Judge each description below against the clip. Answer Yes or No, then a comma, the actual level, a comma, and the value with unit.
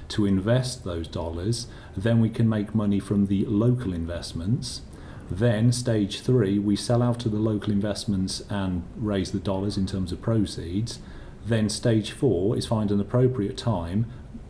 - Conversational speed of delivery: Yes, average, 160 wpm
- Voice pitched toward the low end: Yes, low, 105 Hz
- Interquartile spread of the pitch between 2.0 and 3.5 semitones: Yes, average, 3.1 semitones